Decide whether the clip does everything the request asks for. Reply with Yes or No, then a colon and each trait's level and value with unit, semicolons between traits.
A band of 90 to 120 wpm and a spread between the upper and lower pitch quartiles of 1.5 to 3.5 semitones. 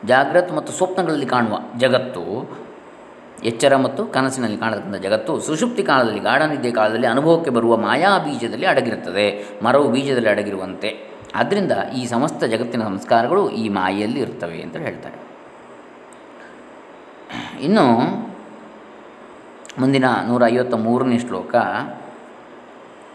Yes: average, 100 wpm; narrow, 2.6 semitones